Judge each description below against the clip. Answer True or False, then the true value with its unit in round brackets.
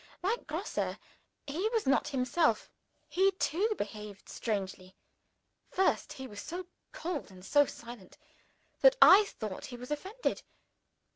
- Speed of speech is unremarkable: False (130 wpm)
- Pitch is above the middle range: True (290 Hz)